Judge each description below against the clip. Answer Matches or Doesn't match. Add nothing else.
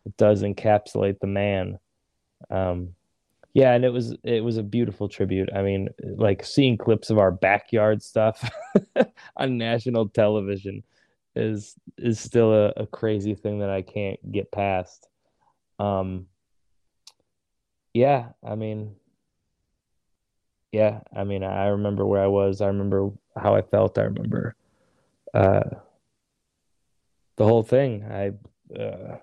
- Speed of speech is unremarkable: Doesn't match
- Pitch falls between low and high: Doesn't match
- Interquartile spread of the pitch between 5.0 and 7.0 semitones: Doesn't match